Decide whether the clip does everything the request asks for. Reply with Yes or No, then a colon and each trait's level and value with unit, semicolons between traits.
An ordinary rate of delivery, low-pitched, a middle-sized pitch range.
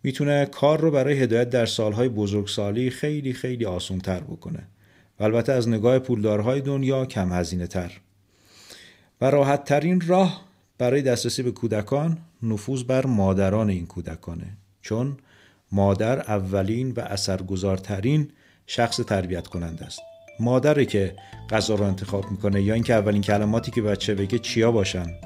Yes: average, 140 wpm; low, 110 Hz; average, 4.8 semitones